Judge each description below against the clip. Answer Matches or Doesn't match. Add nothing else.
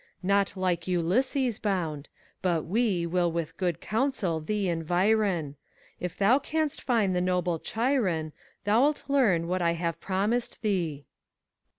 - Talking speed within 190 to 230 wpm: Doesn't match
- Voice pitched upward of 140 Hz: Matches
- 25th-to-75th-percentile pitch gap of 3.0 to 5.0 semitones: Matches